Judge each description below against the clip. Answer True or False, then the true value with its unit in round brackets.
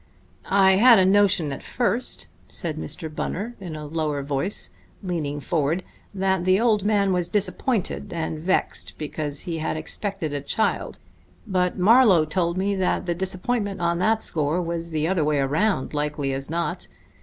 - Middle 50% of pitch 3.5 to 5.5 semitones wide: True (4.2 semitones)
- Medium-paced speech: True (165 wpm)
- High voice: False (175 Hz)